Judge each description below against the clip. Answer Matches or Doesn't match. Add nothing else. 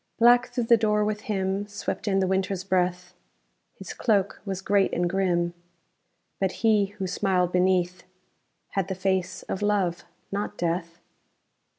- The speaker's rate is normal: Matches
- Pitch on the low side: Doesn't match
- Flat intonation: Matches